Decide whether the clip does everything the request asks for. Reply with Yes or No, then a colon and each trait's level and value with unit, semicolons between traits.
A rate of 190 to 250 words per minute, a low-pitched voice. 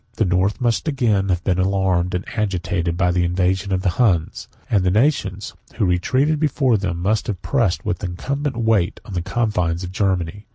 Yes: average, 195 wpm; very low, 95 Hz